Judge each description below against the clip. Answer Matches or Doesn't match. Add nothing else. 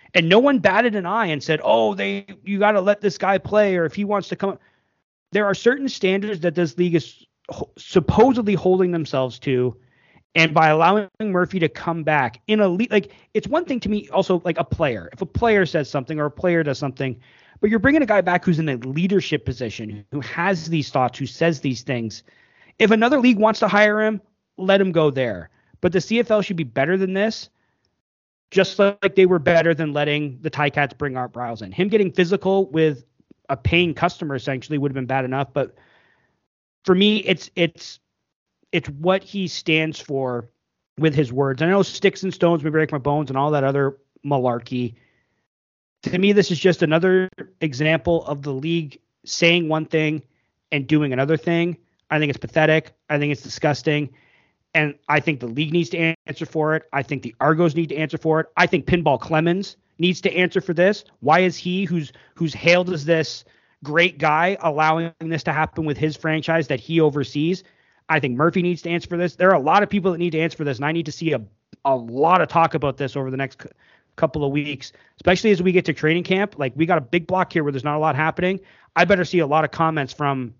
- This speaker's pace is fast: Matches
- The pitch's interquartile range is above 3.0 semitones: Matches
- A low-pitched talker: Doesn't match